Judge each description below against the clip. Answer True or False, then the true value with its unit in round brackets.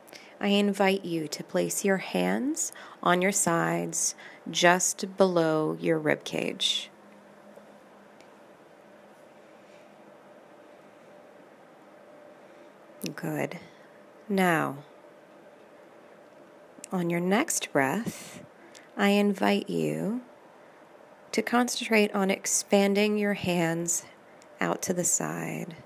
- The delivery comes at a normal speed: False (80 wpm)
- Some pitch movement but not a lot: True (3.7 semitones)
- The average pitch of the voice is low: False (190 Hz)